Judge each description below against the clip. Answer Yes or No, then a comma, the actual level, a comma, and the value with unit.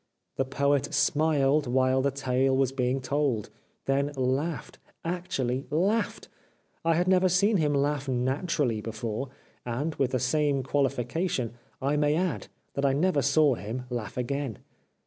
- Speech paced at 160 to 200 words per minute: No, average, 145 wpm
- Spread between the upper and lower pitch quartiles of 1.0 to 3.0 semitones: Yes, average, 2.7 semitones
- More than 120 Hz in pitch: Yes, medium, 140 Hz